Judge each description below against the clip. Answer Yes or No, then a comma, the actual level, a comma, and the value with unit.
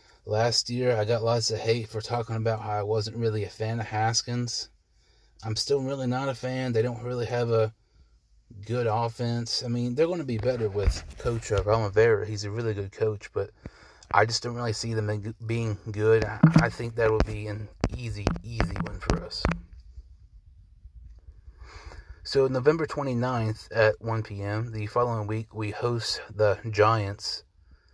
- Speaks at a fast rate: No, average, 170 wpm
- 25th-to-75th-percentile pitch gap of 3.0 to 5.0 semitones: No, narrow, 2.5 semitones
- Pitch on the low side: Yes, low, 110 Hz